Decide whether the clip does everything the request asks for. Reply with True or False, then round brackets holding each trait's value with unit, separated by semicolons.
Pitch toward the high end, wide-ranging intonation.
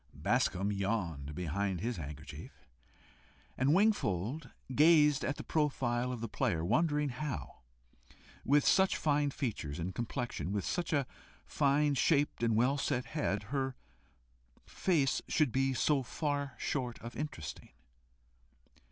False (130 Hz; 6.3 semitones)